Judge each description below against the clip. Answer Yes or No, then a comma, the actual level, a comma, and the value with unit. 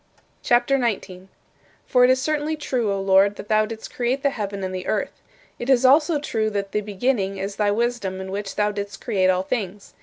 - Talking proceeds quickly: Yes, fast, 215 wpm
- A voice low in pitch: No, high, 210 Hz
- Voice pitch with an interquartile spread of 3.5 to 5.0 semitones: Yes, average, 4.1 semitones